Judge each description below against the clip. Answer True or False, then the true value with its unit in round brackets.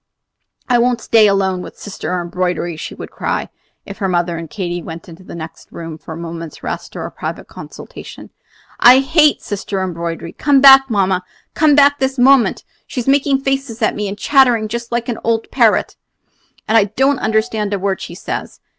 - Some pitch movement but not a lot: False (6.6 semitones)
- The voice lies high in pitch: True (215 Hz)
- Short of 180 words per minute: False (190 wpm)